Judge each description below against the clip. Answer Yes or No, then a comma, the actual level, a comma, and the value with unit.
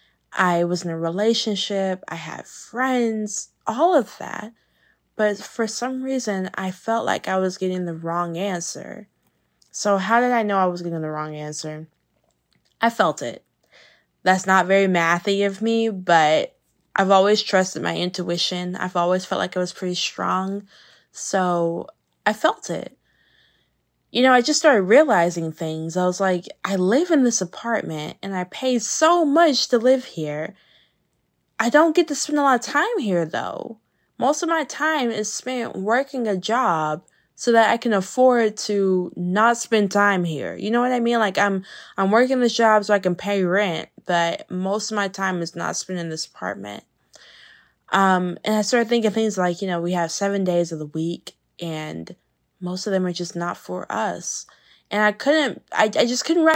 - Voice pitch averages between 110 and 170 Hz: No, high, 195 Hz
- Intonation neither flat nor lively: Yes, average, 4.7 semitones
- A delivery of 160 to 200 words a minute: Yes, average, 185 wpm